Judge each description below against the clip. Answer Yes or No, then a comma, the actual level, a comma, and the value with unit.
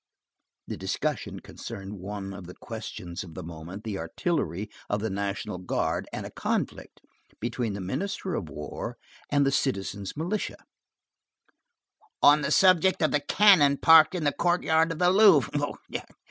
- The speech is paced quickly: No, average, 150 wpm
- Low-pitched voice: Yes, low, 120 Hz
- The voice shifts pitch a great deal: Yes, wide, 9.0 semitones